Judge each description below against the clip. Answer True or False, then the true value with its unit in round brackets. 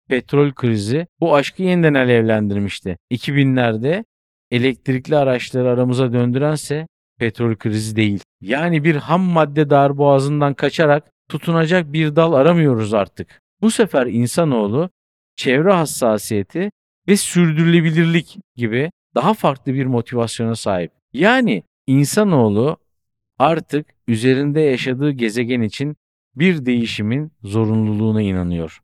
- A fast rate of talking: False (100 wpm)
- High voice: False (135 Hz)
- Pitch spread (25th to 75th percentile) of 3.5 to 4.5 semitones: False (5.3 semitones)